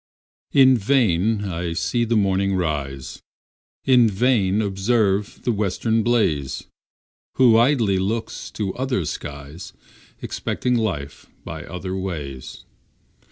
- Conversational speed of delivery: No, slow, 110 wpm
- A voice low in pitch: Yes, low, 100 Hz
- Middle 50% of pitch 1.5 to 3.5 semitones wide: No, average, 4.7 semitones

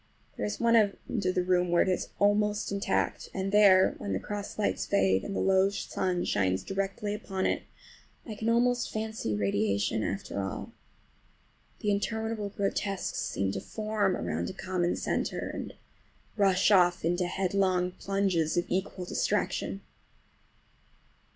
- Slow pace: No, average, 145 wpm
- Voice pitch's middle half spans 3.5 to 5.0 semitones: No, average, 2.9 semitones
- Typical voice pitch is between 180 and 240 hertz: Yes, high, 190 Hz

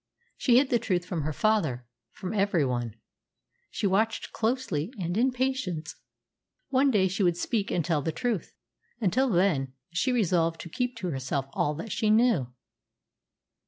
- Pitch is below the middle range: No, high, 190 Hz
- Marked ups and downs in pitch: Yes, wide, 6.3 semitones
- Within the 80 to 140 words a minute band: No, average, 160 wpm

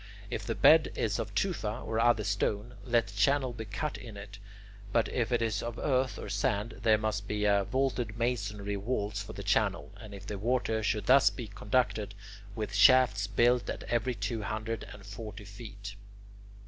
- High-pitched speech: No, low, 110 Hz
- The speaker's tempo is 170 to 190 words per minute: Yes, average, 180 wpm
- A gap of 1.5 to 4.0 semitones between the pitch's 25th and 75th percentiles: Yes, average, 2.9 semitones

